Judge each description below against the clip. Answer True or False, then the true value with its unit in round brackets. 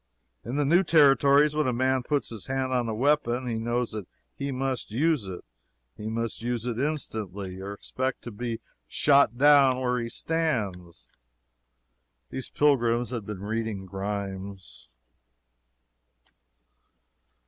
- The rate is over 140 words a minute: False (135 wpm)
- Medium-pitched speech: False (120 Hz)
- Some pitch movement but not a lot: True (4.6 semitones)